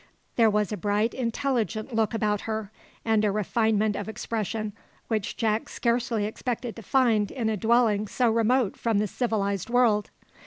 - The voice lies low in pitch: No, high, 220 Hz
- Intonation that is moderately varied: No, narrow, 1.9 semitones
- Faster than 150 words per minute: Yes, average, 160 wpm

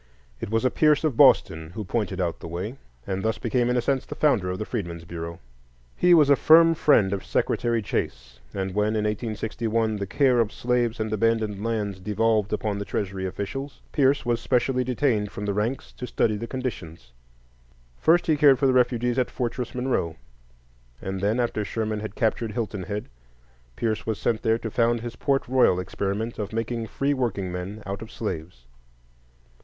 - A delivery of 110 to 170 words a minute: No, average, 185 wpm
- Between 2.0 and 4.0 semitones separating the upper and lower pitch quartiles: Yes, average, 3.6 semitones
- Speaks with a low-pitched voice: Yes, low, 110 Hz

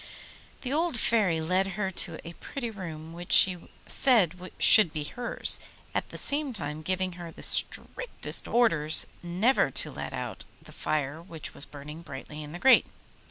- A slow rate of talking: No, average, 165 wpm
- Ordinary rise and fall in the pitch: No, wide, 6.0 semitones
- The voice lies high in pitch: No, medium, 175 Hz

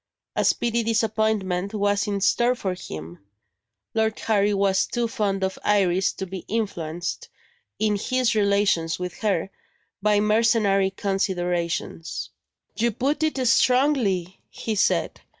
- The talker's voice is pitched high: Yes, high, 205 Hz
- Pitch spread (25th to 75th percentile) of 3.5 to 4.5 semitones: No, average, 2.8 semitones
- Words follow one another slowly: Yes, slow, 125 wpm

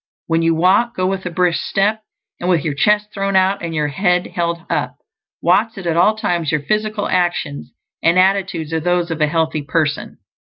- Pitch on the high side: No, medium, 175 Hz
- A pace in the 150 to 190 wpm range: No, average, 200 wpm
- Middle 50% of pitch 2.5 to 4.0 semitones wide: Yes, average, 3.2 semitones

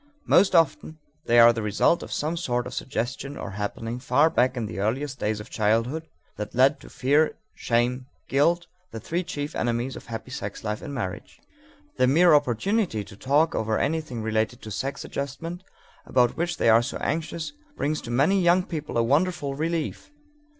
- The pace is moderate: Yes, average, 180 wpm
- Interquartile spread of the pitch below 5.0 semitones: No, wide, 5.6 semitones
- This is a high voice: No, low, 130 Hz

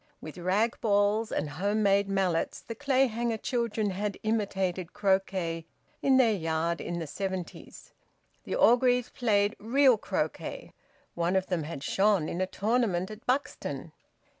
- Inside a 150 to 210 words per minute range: No, average, 140 wpm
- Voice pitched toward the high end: Yes, high, 200 Hz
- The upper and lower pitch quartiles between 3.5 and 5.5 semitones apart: Yes, average, 3.9 semitones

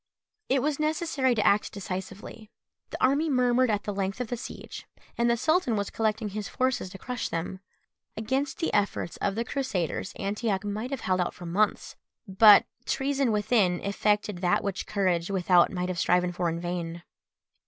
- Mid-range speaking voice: No, high, 210 Hz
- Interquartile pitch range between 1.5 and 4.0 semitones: No, average, 5.0 semitones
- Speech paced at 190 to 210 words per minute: No, average, 175 wpm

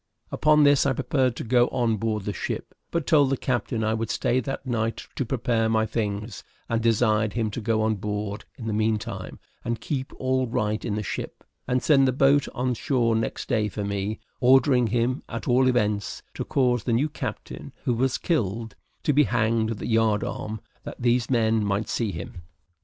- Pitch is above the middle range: No, low, 115 Hz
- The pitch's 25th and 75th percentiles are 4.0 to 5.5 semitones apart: No, average, 2.9 semitones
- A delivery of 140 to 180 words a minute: No, average, 200 wpm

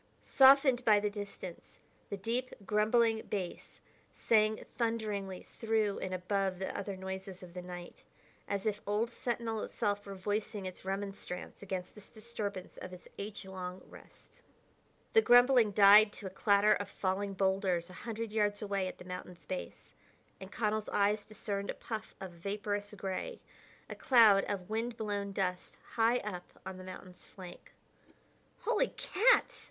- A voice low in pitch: No, high, 205 Hz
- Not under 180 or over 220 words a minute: No, average, 155 wpm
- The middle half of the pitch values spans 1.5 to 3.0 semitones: Yes, narrow, 2.5 semitones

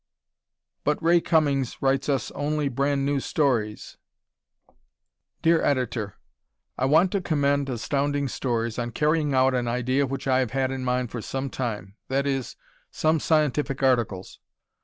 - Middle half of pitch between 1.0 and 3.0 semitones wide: Yes, narrow, 2.5 semitones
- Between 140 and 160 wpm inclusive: Yes, average, 145 wpm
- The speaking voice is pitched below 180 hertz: Yes, low, 135 Hz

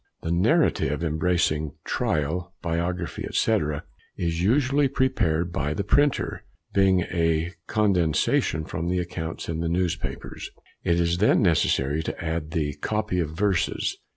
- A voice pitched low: Yes, very low, 85 Hz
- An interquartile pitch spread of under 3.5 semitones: Yes, average, 3.0 semitones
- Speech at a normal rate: No, slow, 130 wpm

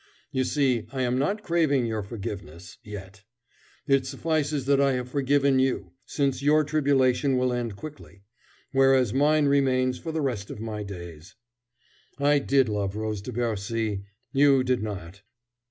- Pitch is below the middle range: Yes, low, 130 Hz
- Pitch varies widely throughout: No, average, 4.9 semitones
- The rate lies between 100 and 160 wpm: Yes, average, 155 wpm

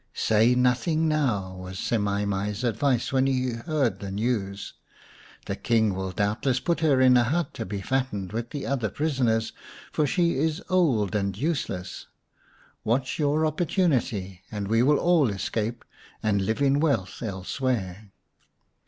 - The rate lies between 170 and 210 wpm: No, average, 155 wpm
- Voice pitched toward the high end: No, low, 120 Hz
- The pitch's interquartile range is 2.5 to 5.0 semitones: No, wide, 5.6 semitones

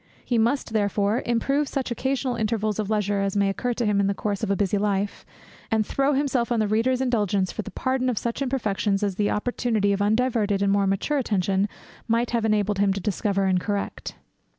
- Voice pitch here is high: Yes, high, 215 Hz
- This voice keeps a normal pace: No, fast, 210 wpm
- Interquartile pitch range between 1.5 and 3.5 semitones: Yes, average, 3.1 semitones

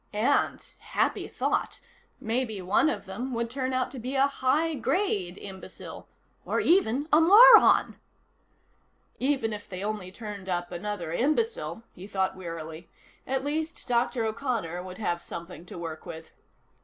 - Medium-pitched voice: No, high, 220 Hz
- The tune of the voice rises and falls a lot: Yes, wide, 6.6 semitones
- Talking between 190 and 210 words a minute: No, average, 145 wpm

